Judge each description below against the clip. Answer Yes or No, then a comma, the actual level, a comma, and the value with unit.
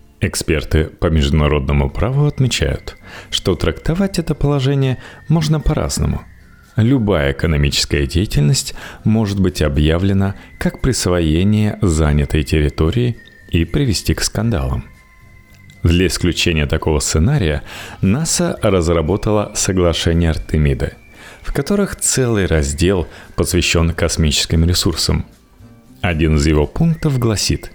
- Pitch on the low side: Yes, very low, 90 Hz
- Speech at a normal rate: No, slow, 95 wpm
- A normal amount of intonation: No, wide, 6.4 semitones